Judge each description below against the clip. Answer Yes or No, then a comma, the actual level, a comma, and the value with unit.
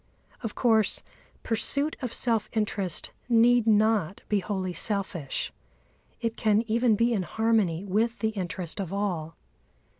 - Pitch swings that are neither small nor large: Yes, average, 3.1 semitones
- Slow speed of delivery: Yes, slow, 130 wpm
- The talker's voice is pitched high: Yes, high, 215 Hz